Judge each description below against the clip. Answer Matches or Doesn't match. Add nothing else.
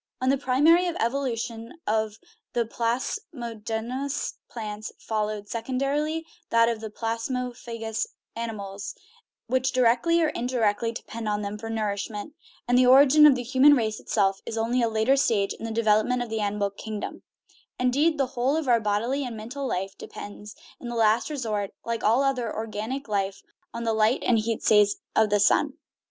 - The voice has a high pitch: Matches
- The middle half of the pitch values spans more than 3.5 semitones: Doesn't match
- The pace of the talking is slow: Doesn't match